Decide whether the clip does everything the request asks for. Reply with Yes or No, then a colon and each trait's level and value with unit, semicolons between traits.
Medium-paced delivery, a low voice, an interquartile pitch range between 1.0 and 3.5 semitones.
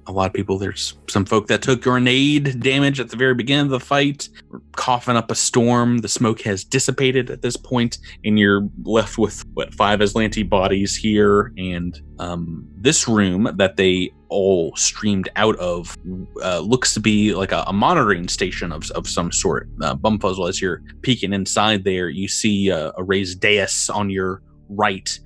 No: average, 185 wpm; low, 105 Hz; average, 4.2 semitones